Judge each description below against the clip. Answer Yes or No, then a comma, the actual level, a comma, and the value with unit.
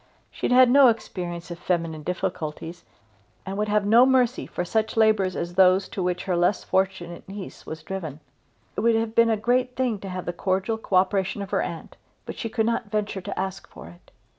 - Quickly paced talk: Yes, fast, 215 wpm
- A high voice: Yes, high, 195 Hz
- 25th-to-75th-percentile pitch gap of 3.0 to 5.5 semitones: Yes, average, 3.9 semitones